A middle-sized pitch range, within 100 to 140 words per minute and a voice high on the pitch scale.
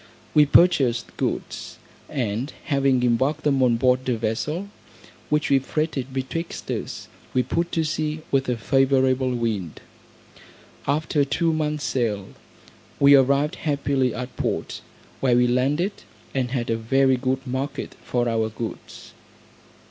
No: average, 3.1 semitones; slow, 135 wpm; low, 130 Hz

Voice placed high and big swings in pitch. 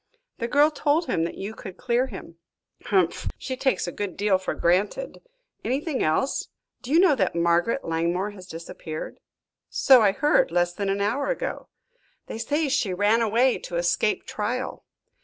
Yes: high, 210 Hz; wide, 6.9 semitones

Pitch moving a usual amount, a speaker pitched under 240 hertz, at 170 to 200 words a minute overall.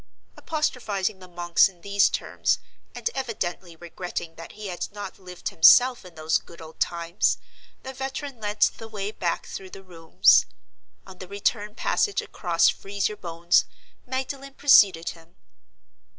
No: average, 4.1 semitones; high, 190 Hz; average, 150 wpm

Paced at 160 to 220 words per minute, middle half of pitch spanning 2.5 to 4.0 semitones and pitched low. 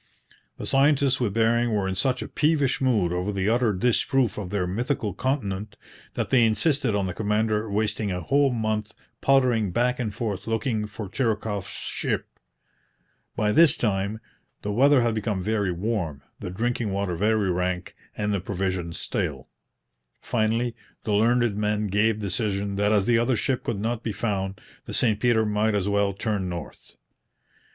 Yes: average, 165 wpm; average, 3.0 semitones; low, 110 Hz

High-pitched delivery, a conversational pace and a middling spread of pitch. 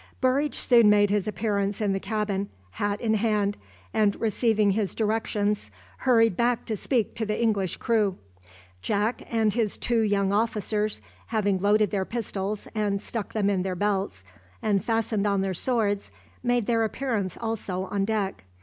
No: high, 210 Hz; average, 160 wpm; narrow, 2.1 semitones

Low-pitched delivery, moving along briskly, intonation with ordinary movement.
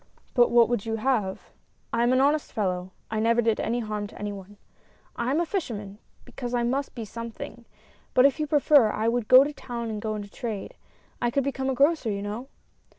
No: high, 235 Hz; fast, 220 wpm; average, 3.7 semitones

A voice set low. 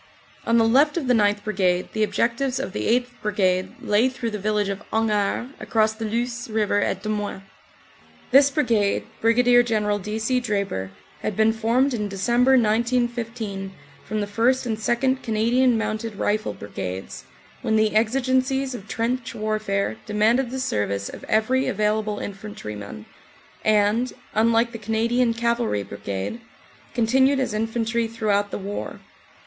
No: high, 220 Hz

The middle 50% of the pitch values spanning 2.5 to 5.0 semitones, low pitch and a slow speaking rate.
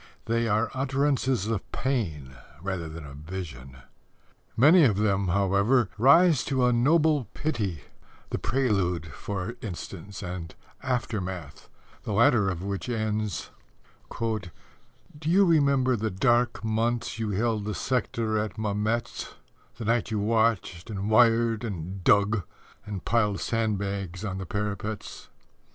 Yes: average, 3.7 semitones; low, 110 Hz; slow, 125 wpm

